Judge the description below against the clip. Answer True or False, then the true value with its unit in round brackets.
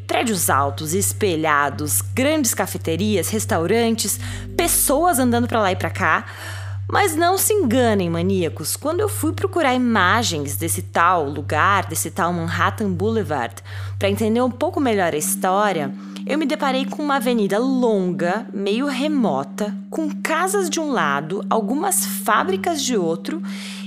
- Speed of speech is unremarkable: True (140 wpm)